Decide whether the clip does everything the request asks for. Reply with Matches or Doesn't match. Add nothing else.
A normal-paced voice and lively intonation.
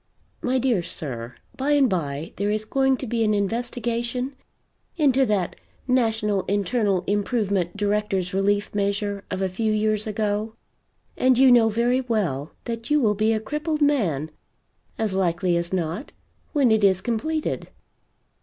Doesn't match